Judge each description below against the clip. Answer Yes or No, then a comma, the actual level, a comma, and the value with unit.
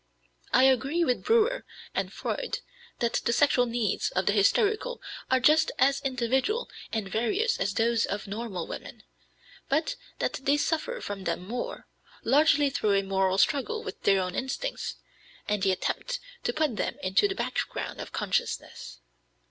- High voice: Yes, very high, 250 Hz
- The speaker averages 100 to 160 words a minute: Yes, average, 155 wpm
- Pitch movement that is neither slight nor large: No, wide, 7.7 semitones